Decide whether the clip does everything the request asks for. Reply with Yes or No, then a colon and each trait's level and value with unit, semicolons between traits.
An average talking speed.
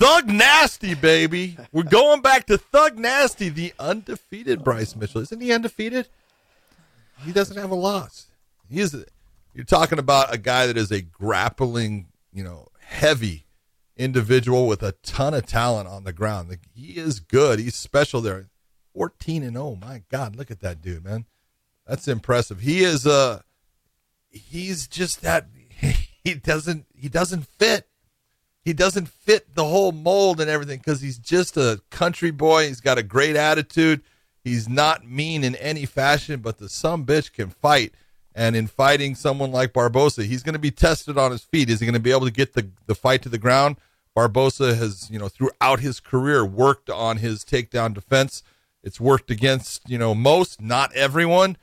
Yes: average, 180 wpm